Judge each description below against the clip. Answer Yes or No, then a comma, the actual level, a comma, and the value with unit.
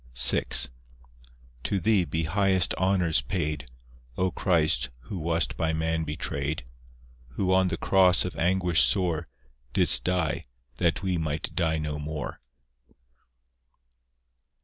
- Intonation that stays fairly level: No, average, 3.1 semitones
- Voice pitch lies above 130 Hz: No, very low, 85 Hz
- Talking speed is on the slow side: Yes, slow, 120 wpm